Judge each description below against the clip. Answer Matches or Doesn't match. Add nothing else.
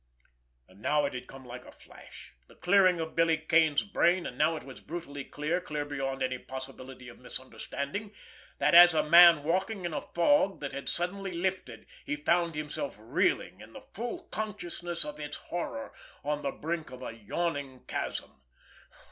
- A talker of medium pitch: Matches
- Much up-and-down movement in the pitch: Doesn't match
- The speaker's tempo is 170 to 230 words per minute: Matches